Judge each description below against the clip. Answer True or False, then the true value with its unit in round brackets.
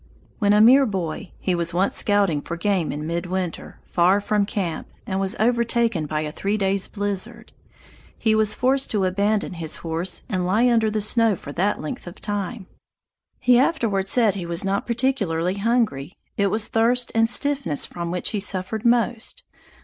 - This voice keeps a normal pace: True (175 wpm)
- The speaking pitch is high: True (200 Hz)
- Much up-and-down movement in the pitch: False (4.1 semitones)